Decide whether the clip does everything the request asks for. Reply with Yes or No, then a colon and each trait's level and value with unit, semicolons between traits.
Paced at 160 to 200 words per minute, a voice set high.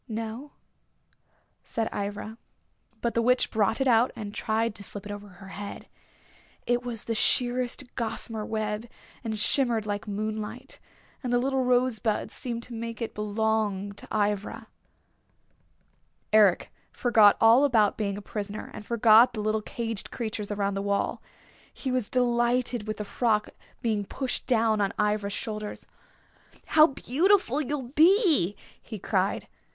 No: average, 145 wpm; high, 220 Hz